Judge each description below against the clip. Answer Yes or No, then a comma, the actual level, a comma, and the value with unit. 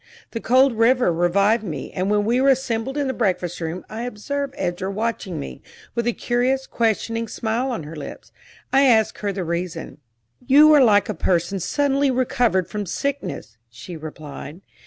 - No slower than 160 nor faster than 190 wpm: Yes, average, 175 wpm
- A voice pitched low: No, high, 220 Hz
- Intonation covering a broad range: Yes, wide, 6.3 semitones